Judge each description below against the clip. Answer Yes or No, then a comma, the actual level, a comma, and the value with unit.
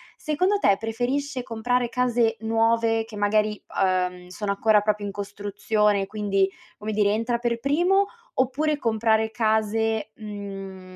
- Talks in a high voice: Yes, high, 220 Hz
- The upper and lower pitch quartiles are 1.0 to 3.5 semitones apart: Yes, narrow, 2.6 semitones